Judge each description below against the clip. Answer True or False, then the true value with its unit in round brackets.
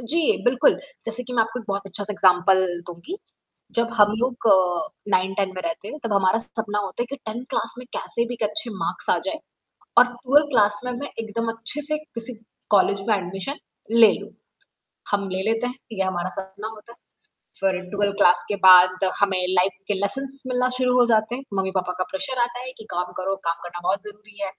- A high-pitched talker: True (210 Hz)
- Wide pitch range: False (4.2 semitones)